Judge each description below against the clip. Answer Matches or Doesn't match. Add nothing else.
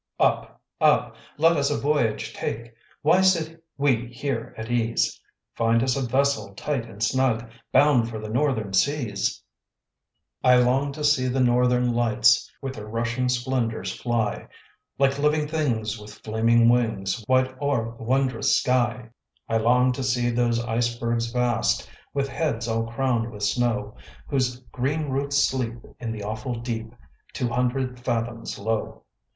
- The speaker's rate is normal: Matches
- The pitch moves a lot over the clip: Doesn't match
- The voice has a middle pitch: Doesn't match